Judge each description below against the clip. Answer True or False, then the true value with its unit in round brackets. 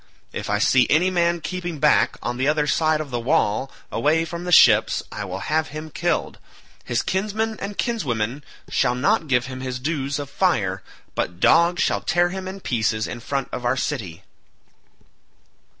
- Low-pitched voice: False (145 Hz)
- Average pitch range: False (6.1 semitones)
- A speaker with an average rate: True (175 wpm)